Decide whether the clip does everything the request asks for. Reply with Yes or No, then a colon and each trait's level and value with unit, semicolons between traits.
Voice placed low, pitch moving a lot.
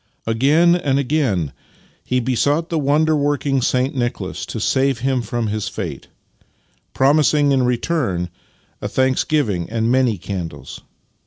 No: low, 130 Hz; average, 4.2 semitones